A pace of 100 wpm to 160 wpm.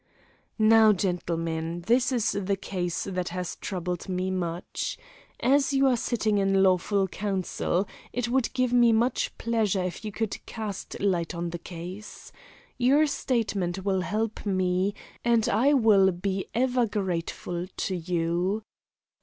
Yes: average, 140 wpm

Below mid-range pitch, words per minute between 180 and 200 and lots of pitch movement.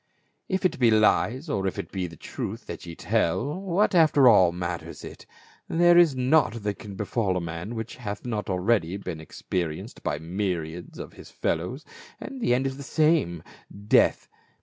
Yes: low, 105 Hz; average, 185 wpm; wide, 7.4 semitones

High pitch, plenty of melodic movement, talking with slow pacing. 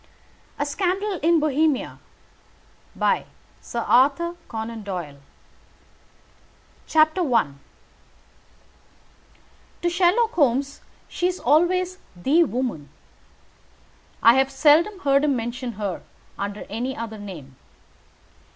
Yes: very high, 275 Hz; wide, 7.3 semitones; slow, 90 wpm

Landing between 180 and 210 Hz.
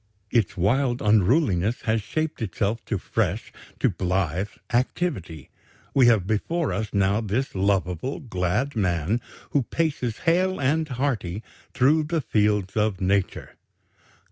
No: low, 110 Hz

